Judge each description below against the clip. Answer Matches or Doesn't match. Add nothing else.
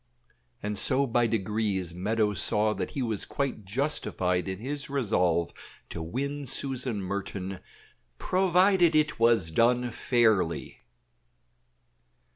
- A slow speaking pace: Matches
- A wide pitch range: Matches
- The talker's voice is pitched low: Matches